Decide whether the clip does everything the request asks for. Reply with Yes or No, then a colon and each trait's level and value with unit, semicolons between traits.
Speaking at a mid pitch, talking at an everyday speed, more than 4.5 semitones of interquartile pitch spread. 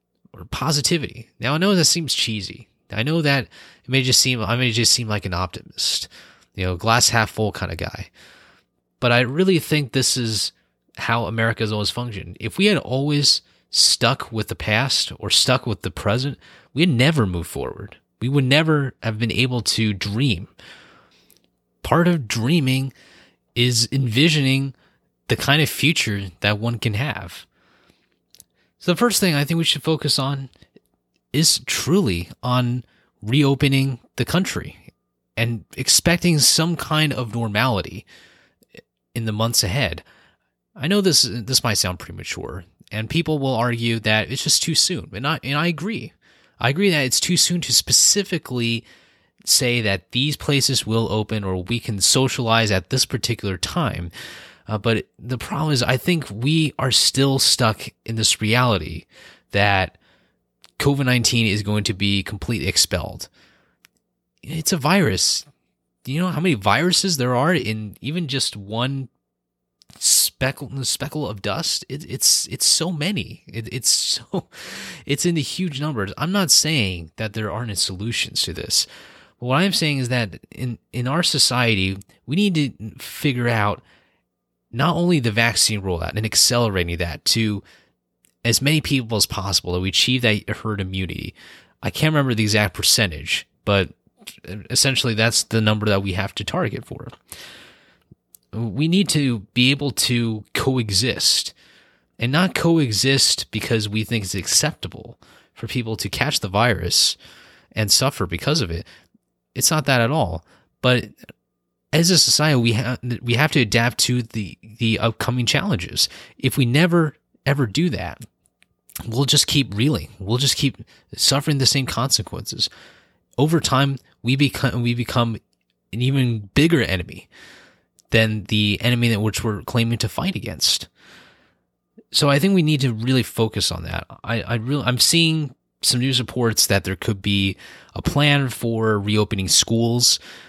No: low, 120 Hz; average, 160 wpm; average, 4.9 semitones